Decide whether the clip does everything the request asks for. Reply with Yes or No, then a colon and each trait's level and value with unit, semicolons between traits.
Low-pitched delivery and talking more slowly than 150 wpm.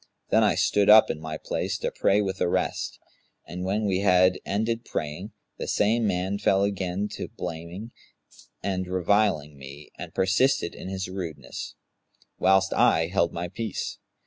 No: very low, 95 Hz; average, 165 wpm